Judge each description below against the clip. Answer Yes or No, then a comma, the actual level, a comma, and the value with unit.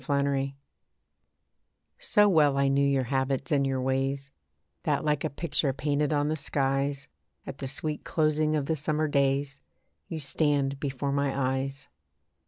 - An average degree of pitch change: No, narrow, 1.6 semitones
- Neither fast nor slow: Yes, average, 150 wpm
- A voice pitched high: No, medium, 140 Hz